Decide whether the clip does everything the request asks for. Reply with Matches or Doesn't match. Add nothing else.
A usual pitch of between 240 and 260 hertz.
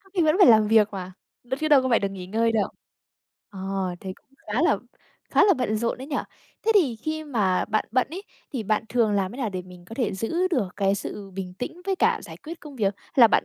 Doesn't match